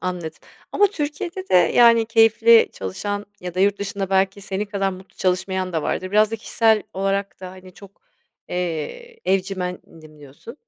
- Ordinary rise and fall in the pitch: Yes, average, 3.5 semitones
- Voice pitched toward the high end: Yes, high, 195 Hz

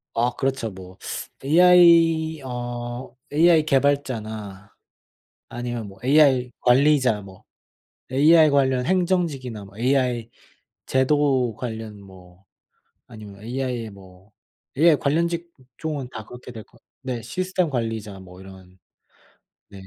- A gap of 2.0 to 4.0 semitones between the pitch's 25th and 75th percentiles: No, average, 5.2 semitones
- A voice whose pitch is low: Yes, low, 125 Hz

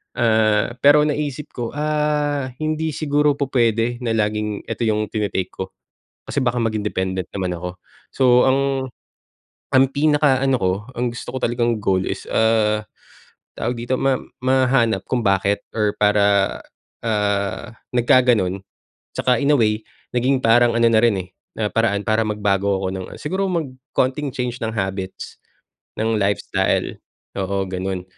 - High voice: No, low, 115 Hz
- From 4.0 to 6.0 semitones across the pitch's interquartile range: Yes, average, 4.3 semitones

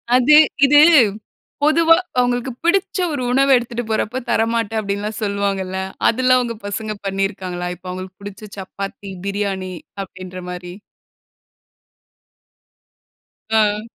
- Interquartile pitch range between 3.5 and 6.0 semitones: Yes, average, 4.2 semitones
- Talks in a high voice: Yes, high, 210 Hz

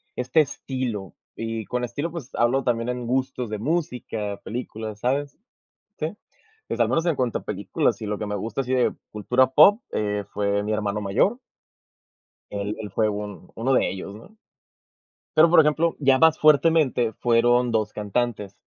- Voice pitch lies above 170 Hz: No, low, 120 Hz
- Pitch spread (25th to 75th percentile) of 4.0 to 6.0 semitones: Yes, average, 4.4 semitones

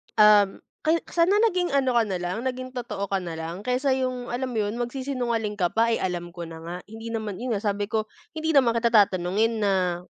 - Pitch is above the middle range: Yes, high, 225 Hz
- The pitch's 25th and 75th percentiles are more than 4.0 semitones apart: Yes, average, 4.7 semitones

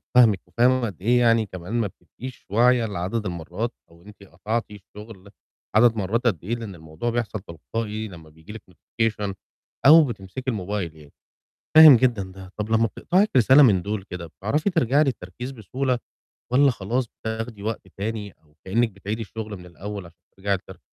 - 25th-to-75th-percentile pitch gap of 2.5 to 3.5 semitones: No, average, 4.0 semitones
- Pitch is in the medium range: No, low, 105 Hz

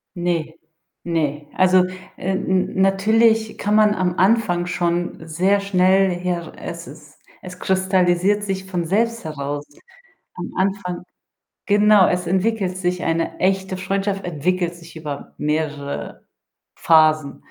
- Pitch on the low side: No, medium, 180 Hz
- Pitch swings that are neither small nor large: No, narrow, 2.3 semitones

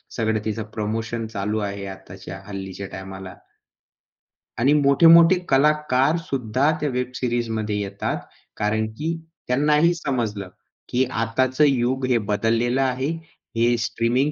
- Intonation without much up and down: No, average, 4.2 semitones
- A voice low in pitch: Yes, low, 120 Hz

